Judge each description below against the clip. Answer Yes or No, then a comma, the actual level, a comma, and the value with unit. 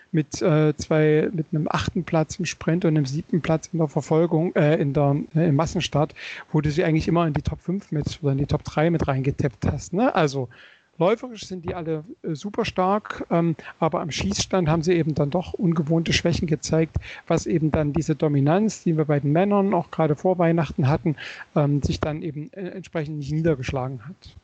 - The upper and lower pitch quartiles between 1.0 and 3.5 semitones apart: Yes, narrow, 2.4 semitones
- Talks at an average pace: No, fast, 205 wpm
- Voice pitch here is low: No, medium, 160 Hz